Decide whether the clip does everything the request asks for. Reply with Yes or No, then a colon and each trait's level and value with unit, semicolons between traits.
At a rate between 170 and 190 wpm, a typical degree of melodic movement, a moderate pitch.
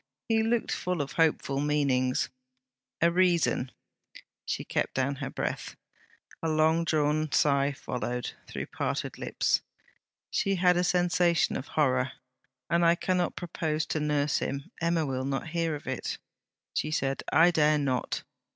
No: average, 140 wpm; average, 3.7 semitones; medium, 155 Hz